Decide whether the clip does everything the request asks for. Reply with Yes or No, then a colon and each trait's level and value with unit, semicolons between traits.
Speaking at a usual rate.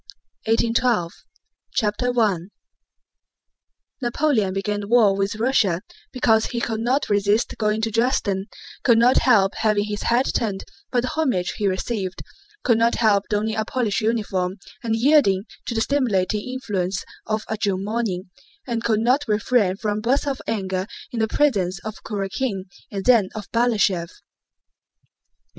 Yes: average, 150 wpm